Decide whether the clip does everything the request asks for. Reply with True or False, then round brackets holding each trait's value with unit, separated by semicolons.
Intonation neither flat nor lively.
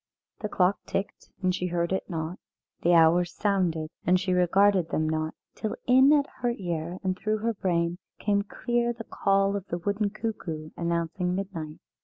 True (3.3 semitones)